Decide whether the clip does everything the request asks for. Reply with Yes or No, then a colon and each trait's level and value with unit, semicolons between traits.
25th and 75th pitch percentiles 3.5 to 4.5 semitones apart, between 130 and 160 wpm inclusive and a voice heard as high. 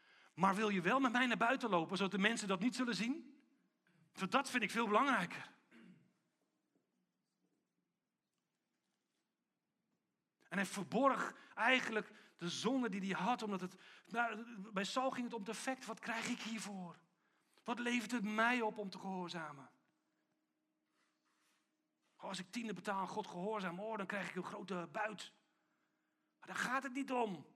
Yes: average, 3.8 semitones; average, 150 wpm; high, 215 Hz